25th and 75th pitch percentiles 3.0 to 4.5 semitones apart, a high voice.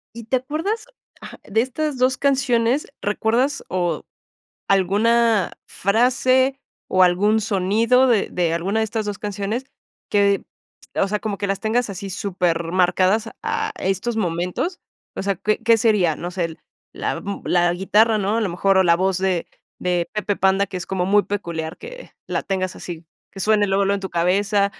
Yes: average, 3.6 semitones; high, 200 Hz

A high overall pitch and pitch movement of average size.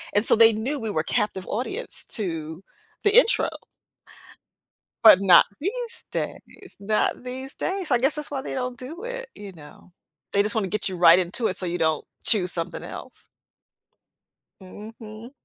No: high, 220 Hz; wide, 6.6 semitones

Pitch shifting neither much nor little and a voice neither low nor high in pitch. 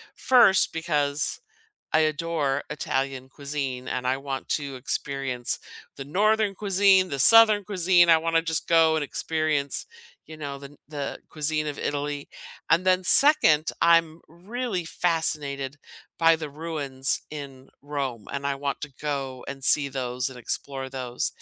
Yes: average, 3.4 semitones; medium, 150 Hz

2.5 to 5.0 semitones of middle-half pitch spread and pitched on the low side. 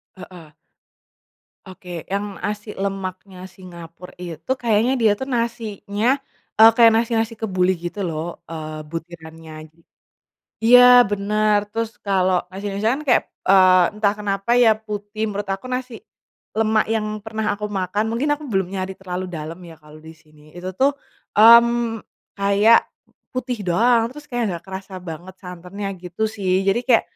No: average, 3.7 semitones; high, 200 Hz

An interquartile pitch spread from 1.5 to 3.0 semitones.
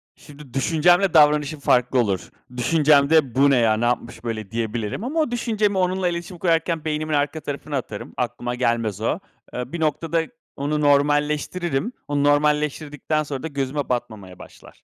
No: average, 4.6 semitones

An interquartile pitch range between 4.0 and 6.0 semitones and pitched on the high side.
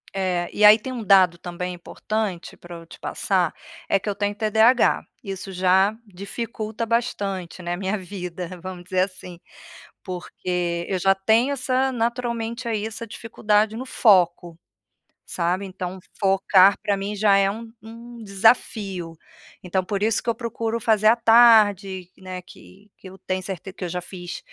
No: average, 3.4 semitones; high, 195 Hz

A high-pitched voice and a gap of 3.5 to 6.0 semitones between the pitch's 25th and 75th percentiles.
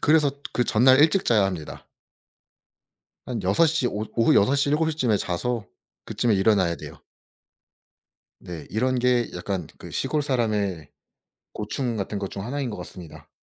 No: low, 115 Hz; average, 5.1 semitones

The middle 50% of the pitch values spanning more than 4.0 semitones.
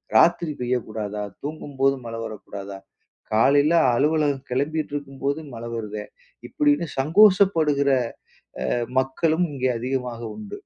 Yes: average, 4.6 semitones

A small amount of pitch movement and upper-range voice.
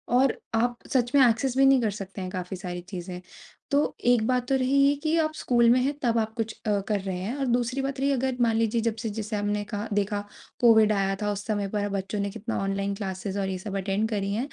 No: average, 3.7 semitones; high, 215 Hz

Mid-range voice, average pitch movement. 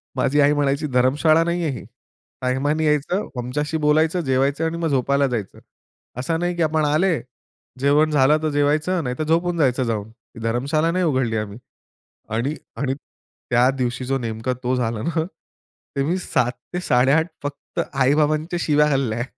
Yes: medium, 145 Hz; average, 3.8 semitones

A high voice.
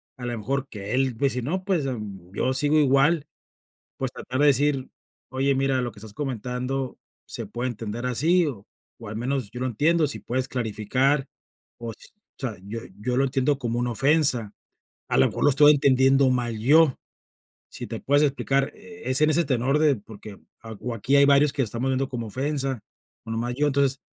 No: low, 130 Hz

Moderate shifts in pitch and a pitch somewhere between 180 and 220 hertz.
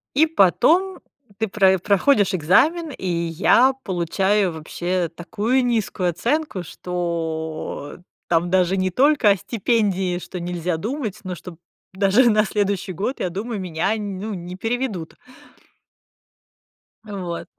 Yes: average, 4.2 semitones; high, 190 Hz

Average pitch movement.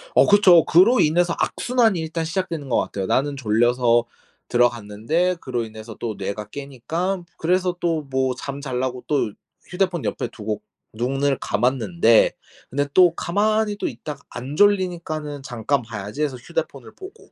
No: wide, 6.6 semitones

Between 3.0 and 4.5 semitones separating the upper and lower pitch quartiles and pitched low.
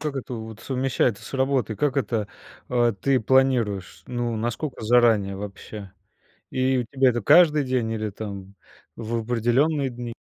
Yes: average, 3.3 semitones; low, 120 Hz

